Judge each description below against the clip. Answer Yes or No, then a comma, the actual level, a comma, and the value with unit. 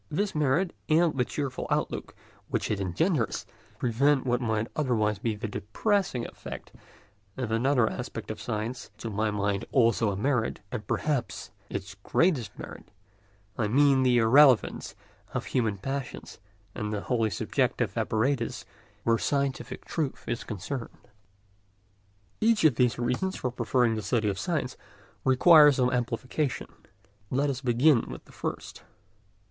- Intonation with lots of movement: No, average, 4.3 semitones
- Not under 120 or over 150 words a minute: Yes, average, 140 wpm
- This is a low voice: Yes, low, 125 Hz